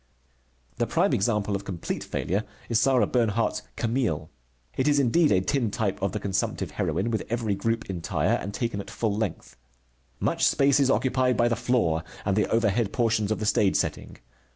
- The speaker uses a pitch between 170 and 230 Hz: No, low, 110 Hz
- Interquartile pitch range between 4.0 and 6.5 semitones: No, average, 3.3 semitones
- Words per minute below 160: No, average, 175 wpm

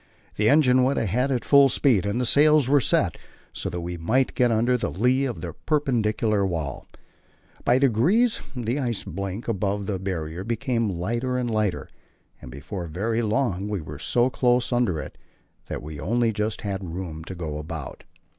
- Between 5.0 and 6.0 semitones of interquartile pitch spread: Yes, average, 5.3 semitones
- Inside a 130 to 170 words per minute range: No, average, 180 wpm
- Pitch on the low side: Yes, low, 110 Hz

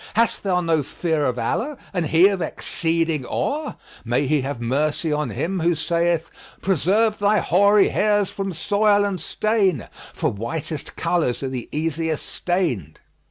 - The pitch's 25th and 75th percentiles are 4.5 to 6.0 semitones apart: Yes, average, 5.1 semitones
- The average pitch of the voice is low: No, medium, 170 Hz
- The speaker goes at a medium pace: Yes, average, 160 wpm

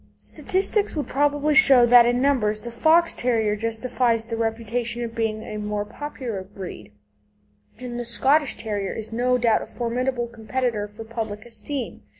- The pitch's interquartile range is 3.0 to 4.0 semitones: No, narrow, 2.4 semitones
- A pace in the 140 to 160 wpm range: Yes, average, 155 wpm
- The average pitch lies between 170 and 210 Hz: No, high, 235 Hz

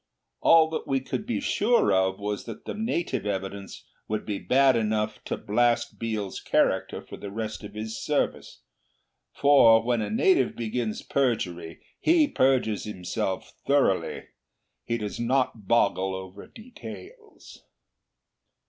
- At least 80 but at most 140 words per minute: Yes, slow, 135 wpm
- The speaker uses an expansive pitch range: No, average, 4.6 semitones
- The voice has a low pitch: Yes, low, 110 Hz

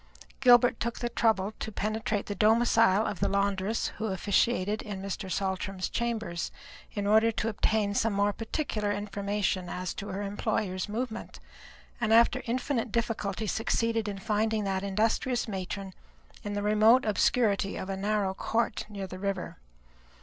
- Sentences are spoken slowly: No, average, 150 wpm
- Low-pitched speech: No, high, 210 Hz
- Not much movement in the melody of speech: Yes, narrow, 2.3 semitones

